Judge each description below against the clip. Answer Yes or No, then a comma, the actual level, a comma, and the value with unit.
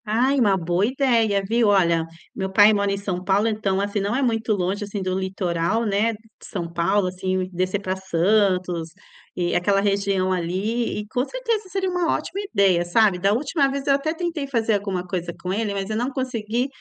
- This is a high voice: Yes, high, 200 Hz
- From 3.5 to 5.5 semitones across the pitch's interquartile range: Yes, average, 3.8 semitones